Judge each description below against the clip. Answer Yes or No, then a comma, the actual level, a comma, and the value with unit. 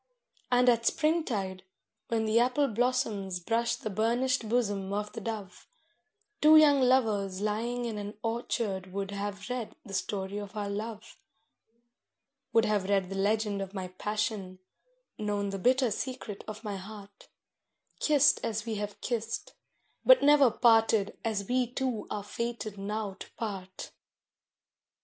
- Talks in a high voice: Yes, high, 215 Hz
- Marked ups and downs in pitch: No, average, 3.0 semitones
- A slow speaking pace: No, average, 145 wpm